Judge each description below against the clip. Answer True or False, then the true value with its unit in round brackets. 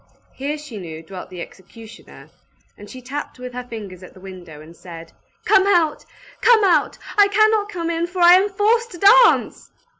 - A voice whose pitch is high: True (270 Hz)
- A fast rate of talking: False (185 wpm)